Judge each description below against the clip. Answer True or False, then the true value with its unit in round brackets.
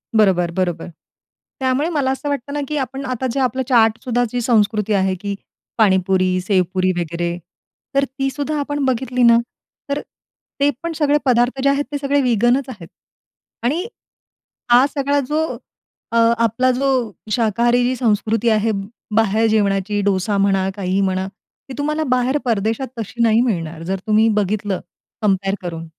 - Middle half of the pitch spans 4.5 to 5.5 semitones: True (5.1 semitones)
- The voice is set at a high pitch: True (225 Hz)